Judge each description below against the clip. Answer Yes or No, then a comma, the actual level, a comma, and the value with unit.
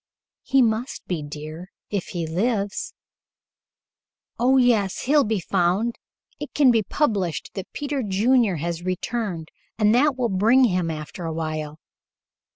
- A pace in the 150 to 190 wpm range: No, average, 140 wpm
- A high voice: Yes, high, 200 Hz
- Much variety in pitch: Yes, wide, 6.0 semitones